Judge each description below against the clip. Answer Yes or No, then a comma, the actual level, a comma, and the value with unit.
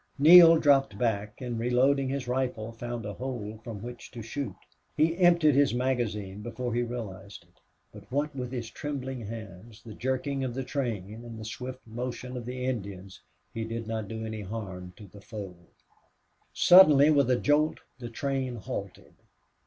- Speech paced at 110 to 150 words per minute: No, average, 170 wpm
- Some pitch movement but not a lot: Yes, average, 3.4 semitones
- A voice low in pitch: Yes, low, 120 Hz